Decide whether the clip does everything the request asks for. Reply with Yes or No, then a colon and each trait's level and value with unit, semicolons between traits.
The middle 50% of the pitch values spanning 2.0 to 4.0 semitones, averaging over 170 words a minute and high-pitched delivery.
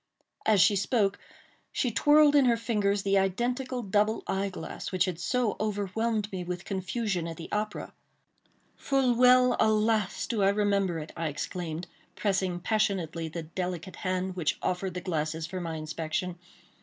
No: average, 3.6 semitones; average, 155 wpm; high, 195 Hz